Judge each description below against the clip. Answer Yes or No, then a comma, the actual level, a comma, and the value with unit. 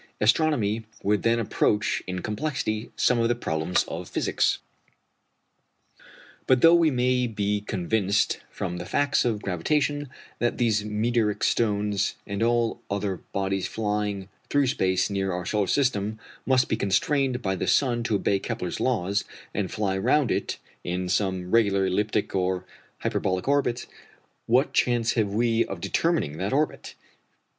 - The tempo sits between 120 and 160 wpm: Yes, average, 145 wpm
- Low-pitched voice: Yes, low, 105 Hz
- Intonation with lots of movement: No, average, 3.8 semitones